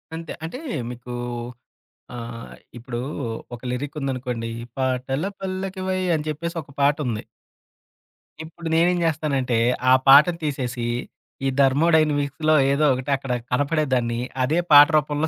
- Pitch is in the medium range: Yes, medium, 145 Hz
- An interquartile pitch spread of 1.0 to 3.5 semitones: No, average, 3.9 semitones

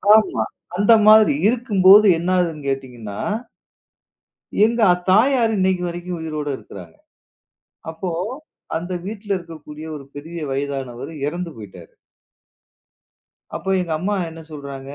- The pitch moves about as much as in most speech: No, wide, 5.7 semitones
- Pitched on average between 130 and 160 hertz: No, medium, 170 Hz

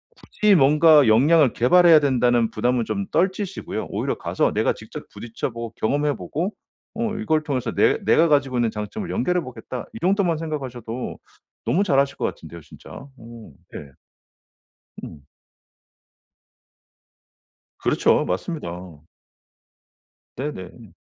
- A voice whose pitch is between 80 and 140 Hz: Yes, low, 135 Hz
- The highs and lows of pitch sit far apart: Yes, wide, 6.2 semitones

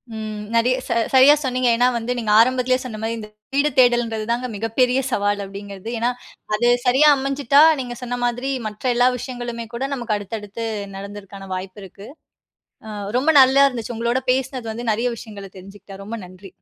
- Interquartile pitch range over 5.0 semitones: No, average, 3.4 semitones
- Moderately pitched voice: No, high, 235 Hz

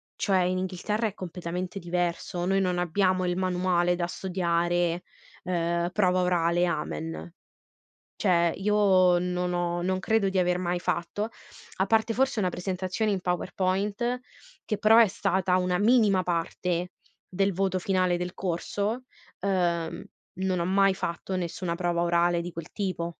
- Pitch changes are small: Yes, narrow, 1.9 semitones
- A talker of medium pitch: Yes, medium, 180 Hz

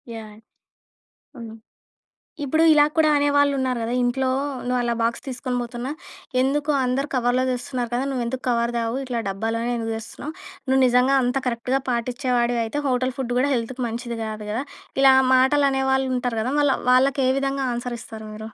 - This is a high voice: Yes, very high, 250 Hz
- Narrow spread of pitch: Yes, narrow, 2.1 semitones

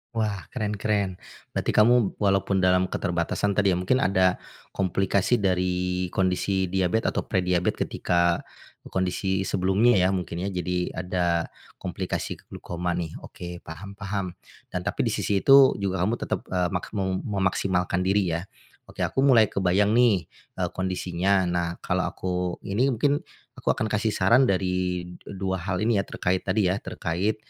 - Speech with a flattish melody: Yes, narrow, 2.1 semitones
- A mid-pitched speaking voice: No, very low, 95 Hz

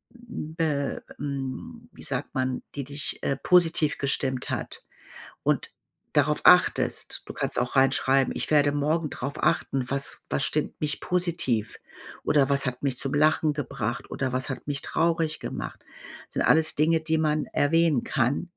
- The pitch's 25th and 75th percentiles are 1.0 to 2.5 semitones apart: No, average, 2.9 semitones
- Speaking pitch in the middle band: Yes, medium, 145 Hz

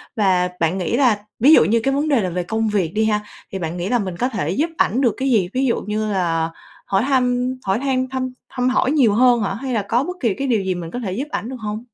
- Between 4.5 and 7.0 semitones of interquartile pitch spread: Yes, average, 5.1 semitones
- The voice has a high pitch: Yes, high, 225 Hz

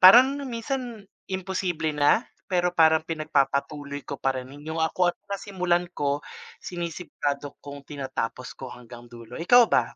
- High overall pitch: No, medium, 160 Hz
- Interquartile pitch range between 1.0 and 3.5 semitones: No, average, 4.7 semitones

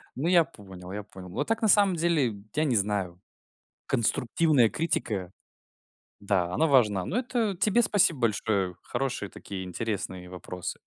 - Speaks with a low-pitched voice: Yes, low, 115 Hz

